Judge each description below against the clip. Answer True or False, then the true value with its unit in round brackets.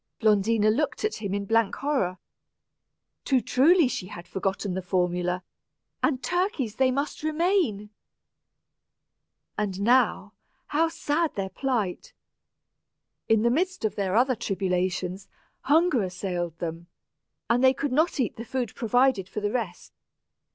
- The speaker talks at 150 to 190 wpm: False (135 wpm)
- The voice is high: True (225 Hz)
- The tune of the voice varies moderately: False (6.3 semitones)